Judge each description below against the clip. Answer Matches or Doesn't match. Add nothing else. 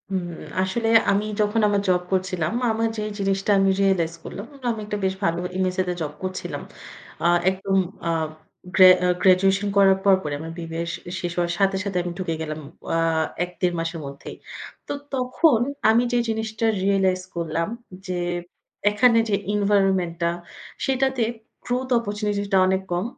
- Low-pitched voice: Doesn't match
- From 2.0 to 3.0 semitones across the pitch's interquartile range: Matches